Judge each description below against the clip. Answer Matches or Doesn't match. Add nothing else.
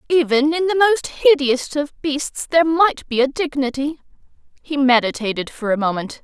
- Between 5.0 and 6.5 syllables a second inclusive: Doesn't match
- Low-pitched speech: Doesn't match